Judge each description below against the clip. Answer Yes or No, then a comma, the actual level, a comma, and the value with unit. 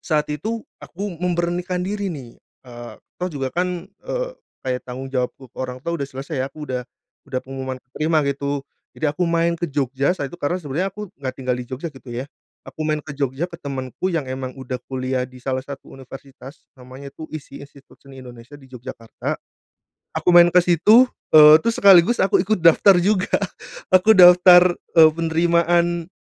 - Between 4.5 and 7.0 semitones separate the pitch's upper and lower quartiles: Yes, average, 5.0 semitones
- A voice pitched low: No, medium, 150 Hz